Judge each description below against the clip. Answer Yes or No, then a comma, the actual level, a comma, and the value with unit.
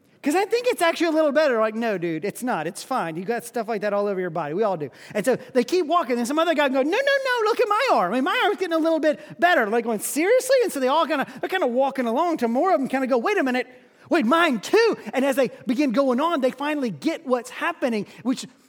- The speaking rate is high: Yes, fast, 295 wpm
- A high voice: Yes, very high, 270 Hz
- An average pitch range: No, wide, 5.8 semitones